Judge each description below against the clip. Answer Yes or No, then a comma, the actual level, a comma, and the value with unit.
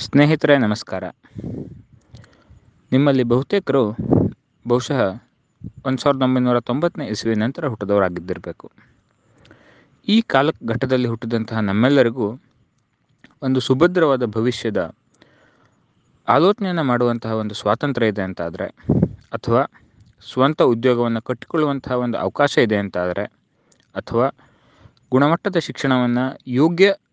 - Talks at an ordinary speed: Yes, average, 80 wpm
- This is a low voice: Yes, low, 125 Hz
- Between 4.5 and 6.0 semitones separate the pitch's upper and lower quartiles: No, average, 4.1 semitones